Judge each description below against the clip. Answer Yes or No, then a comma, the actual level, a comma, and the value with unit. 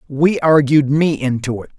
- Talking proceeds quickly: No, average, 170 wpm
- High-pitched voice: No, medium, 145 Hz